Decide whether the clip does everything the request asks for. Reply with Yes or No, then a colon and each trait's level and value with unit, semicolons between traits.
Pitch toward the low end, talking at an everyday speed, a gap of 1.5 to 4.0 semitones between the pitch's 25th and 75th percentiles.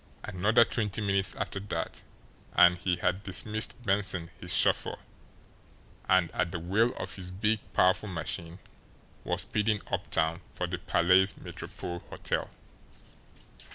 No: very low, 95 Hz; slow, 125 wpm; average, 2.9 semitones